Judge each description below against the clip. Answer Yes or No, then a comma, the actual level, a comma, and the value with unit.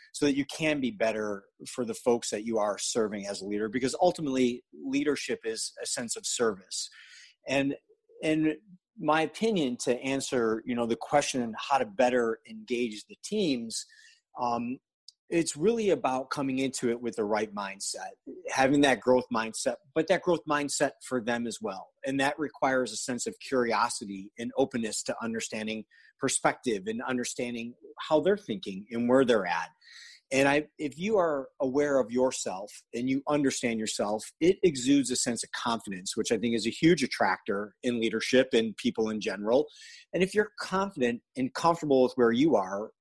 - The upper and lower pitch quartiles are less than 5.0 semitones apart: No, average, 5.3 semitones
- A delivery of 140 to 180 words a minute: Yes, average, 175 wpm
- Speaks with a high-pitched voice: No, low, 135 Hz